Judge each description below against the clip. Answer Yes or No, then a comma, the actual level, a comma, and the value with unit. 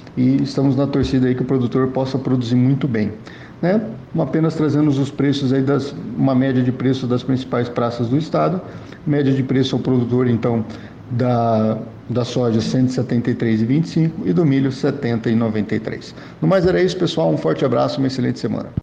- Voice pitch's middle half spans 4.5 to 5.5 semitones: No, narrow, 2.6 semitones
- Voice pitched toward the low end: Yes, low, 130 Hz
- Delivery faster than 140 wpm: Yes, average, 175 wpm